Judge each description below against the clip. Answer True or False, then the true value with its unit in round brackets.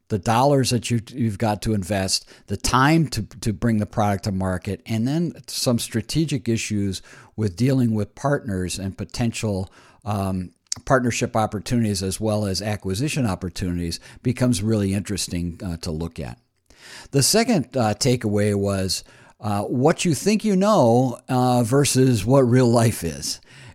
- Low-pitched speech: True (110 Hz)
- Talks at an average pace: True (150 wpm)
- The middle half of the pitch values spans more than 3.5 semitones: True (4.2 semitones)